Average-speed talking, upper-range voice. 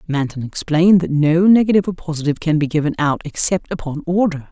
No: average, 185 wpm; medium, 165 Hz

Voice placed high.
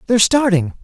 Yes: high, 205 Hz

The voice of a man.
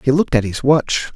Yes: male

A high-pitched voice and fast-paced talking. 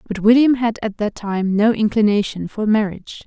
No: high, 210 Hz; average, 185 wpm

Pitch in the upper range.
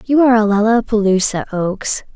Yes: high, 215 Hz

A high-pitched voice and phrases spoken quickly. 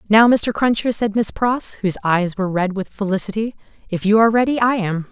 Yes: high, 210 Hz; fast, 210 wpm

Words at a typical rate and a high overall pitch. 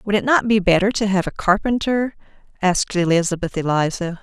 Yes: average, 170 wpm; high, 195 Hz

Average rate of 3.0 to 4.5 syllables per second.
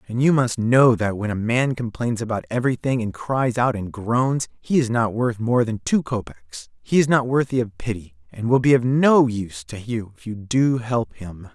No: 4.8 syllables/s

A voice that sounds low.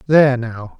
Yes: low, 125 Hz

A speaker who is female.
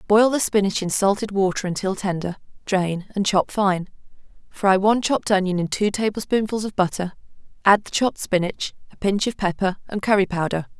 Yes: female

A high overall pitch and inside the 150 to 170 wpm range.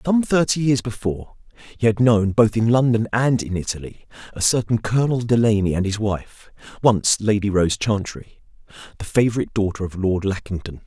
No: low, 110 Hz; average, 165 wpm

